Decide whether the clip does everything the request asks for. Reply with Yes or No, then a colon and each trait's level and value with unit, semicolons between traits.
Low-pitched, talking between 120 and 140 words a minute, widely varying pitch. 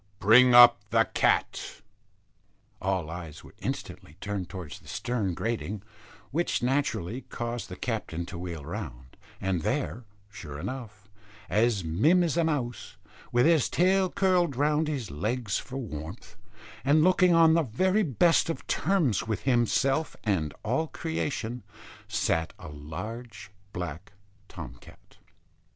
Yes: low, 120 Hz; slow, 135 wpm; wide, 8.4 semitones